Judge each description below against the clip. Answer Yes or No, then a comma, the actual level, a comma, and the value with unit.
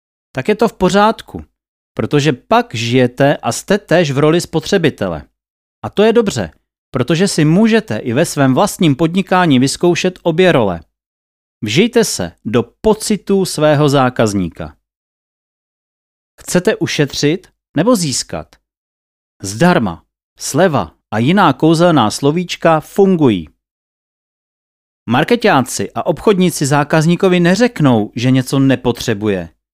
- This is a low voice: No, medium, 150 Hz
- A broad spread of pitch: Yes, wide, 8.4 semitones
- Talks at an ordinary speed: No, slow, 110 wpm